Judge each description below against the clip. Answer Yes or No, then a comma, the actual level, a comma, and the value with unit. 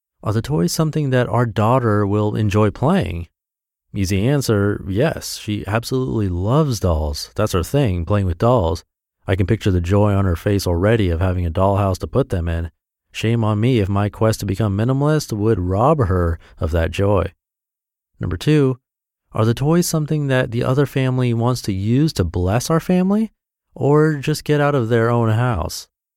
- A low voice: Yes, low, 110 Hz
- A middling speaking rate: Yes, average, 185 wpm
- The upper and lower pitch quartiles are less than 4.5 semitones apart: No, wide, 5.4 semitones